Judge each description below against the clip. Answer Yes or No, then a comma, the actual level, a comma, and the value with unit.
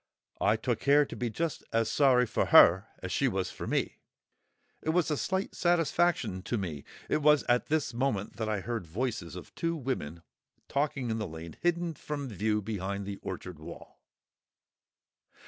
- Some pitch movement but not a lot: No, wide, 7.2 semitones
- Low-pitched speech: Yes, low, 115 Hz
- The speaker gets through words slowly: No, average, 175 wpm